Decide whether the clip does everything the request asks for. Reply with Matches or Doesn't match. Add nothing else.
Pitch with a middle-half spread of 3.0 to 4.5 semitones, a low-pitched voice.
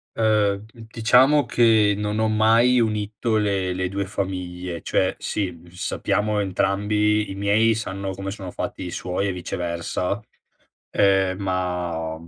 Doesn't match